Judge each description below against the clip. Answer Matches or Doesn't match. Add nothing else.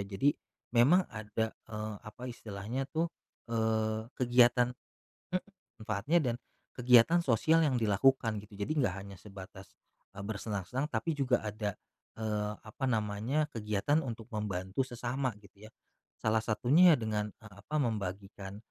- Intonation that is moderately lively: Matches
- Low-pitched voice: Matches